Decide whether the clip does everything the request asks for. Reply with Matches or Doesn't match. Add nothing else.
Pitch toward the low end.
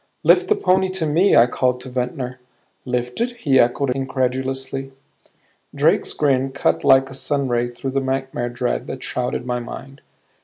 Matches